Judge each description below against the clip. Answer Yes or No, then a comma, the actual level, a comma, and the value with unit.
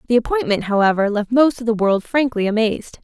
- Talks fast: No, average, 195 wpm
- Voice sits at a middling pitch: No, high, 230 Hz